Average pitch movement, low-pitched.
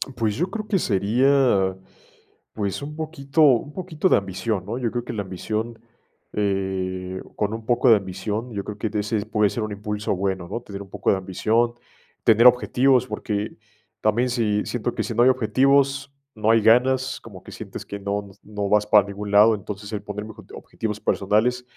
Yes: average, 3.5 semitones; low, 110 Hz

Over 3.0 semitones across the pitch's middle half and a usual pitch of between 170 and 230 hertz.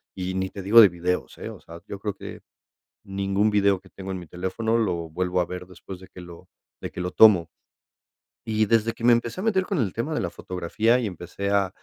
No: average, 3.6 semitones; very low, 95 Hz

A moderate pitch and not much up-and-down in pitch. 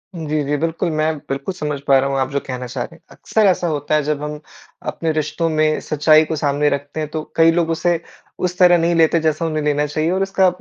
Yes: medium, 155 Hz; narrow, 2.0 semitones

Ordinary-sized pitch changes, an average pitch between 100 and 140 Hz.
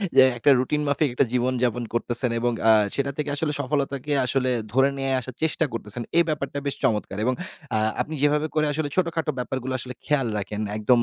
Yes: average, 3.3 semitones; low, 135 Hz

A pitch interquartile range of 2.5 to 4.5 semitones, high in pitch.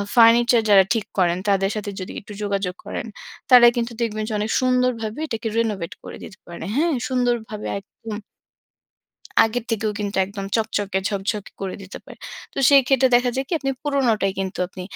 Yes: average, 3.5 semitones; high, 220 Hz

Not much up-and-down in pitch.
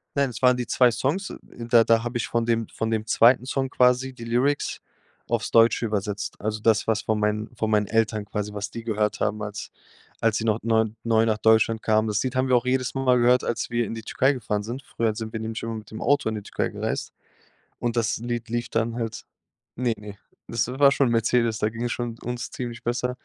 Yes: narrow, 2.0 semitones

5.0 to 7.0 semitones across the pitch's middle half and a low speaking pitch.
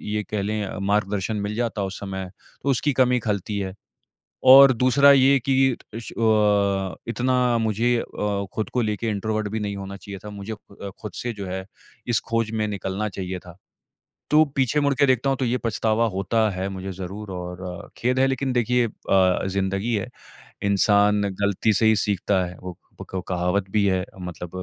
No: average, 3.4 semitones; low, 105 Hz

